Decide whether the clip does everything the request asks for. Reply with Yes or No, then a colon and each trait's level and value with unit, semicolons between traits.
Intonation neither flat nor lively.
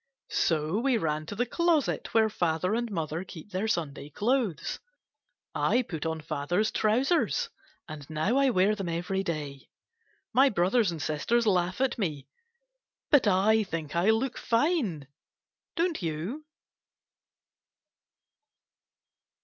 No: wide, 6.8 semitones